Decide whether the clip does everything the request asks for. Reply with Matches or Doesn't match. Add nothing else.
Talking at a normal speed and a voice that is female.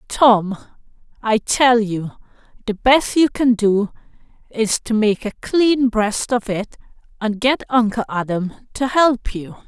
Matches